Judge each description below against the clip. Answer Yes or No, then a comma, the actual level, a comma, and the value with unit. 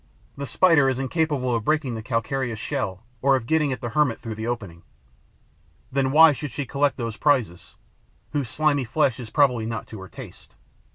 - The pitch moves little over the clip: No, average, 4.1 semitones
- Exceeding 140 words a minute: Yes, average, 185 wpm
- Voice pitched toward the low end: Yes, low, 130 Hz